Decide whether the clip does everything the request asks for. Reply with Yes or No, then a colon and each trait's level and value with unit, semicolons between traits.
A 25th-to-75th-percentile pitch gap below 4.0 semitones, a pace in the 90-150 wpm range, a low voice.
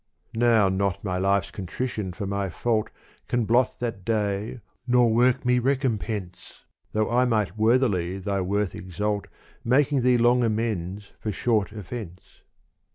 Yes: average, 3.6 semitones; average, 140 wpm; low, 110 Hz